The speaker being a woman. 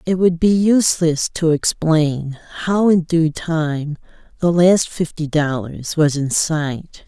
Yes: female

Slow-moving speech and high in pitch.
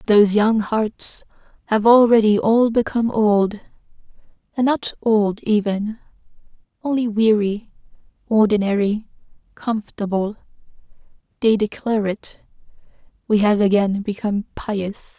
Yes: slow, 85 wpm; high, 215 Hz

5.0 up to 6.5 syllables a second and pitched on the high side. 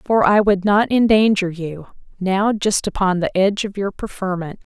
No: 4.8 syllables/s; high, 195 Hz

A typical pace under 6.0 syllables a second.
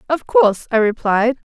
Yes: 5.0 syllables/s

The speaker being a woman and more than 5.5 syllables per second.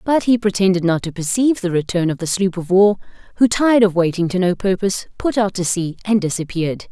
Yes: female; 6.1 syllables/s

